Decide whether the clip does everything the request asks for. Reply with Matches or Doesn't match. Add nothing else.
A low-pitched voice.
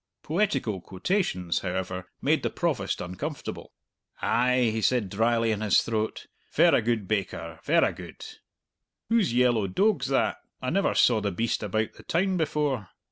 Matches